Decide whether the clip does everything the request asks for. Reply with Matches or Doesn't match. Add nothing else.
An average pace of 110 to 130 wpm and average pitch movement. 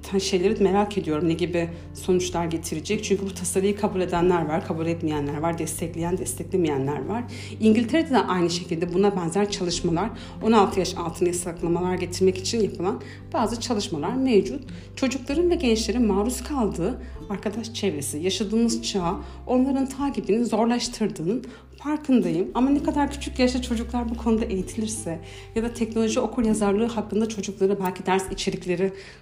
Doesn't match